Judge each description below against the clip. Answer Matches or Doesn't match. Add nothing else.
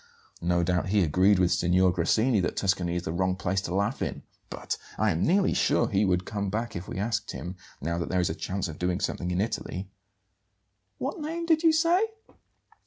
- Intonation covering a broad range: Doesn't match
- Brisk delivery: Matches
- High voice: Doesn't match